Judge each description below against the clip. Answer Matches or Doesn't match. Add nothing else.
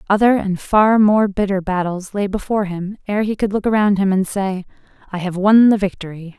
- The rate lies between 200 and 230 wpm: Matches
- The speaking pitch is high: Matches